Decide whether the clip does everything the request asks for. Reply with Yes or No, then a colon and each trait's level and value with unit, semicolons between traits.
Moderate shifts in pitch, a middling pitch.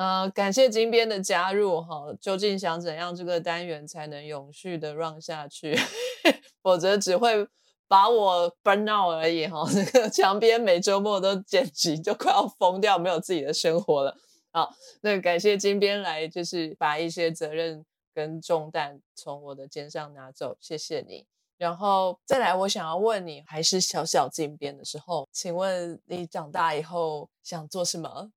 Yes: average, 4.3 semitones; medium, 175 Hz